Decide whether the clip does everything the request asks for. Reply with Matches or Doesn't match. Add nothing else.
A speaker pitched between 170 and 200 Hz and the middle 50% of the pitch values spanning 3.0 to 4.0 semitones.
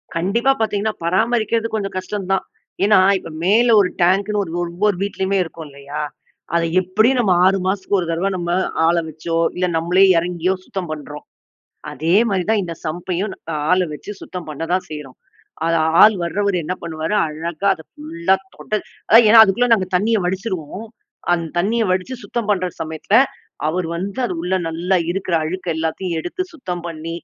Matches